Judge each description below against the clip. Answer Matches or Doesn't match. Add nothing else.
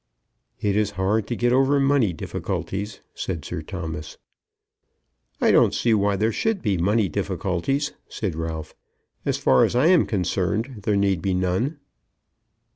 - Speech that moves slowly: Doesn't match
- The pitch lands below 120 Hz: Matches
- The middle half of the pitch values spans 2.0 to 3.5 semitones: Doesn't match